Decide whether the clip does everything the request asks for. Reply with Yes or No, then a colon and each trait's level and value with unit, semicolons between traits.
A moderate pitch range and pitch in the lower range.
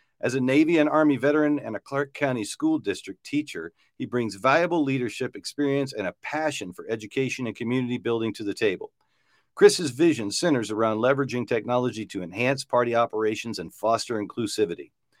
Yes: average, 4.6 semitones; low, 130 Hz